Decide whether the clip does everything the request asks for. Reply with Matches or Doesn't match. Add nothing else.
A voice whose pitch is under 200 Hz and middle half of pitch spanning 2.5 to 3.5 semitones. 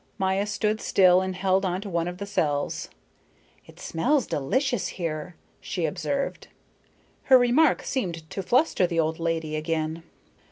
Doesn't match